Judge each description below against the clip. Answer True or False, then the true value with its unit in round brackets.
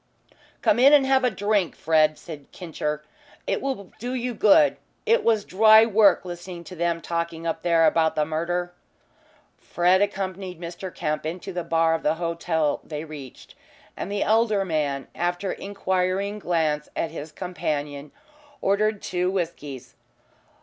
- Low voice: False (175 Hz)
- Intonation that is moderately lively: True (3.8 semitones)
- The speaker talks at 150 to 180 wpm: True (155 wpm)